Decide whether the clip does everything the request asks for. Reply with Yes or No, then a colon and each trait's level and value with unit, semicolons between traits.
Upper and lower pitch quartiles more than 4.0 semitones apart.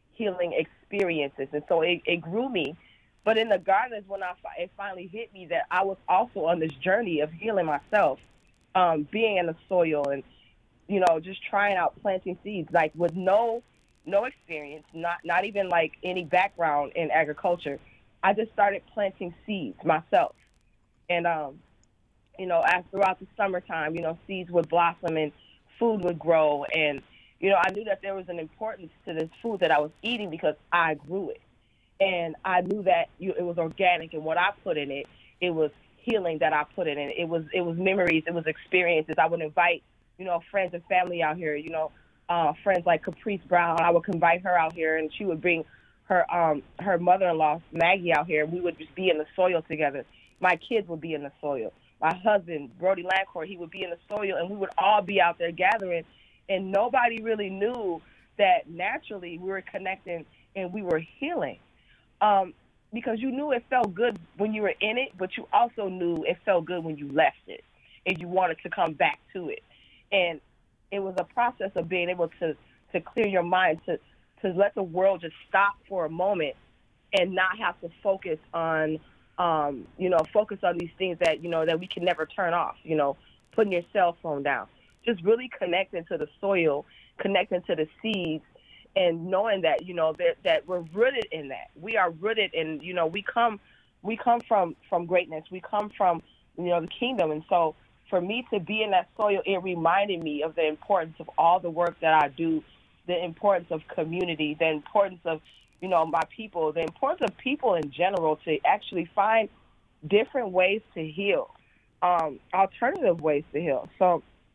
No: average, 3.6 semitones